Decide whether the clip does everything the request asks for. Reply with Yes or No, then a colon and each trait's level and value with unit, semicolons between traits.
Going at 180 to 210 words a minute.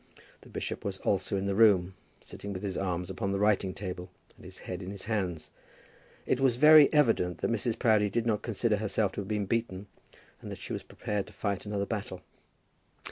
Yes: fast, 205 wpm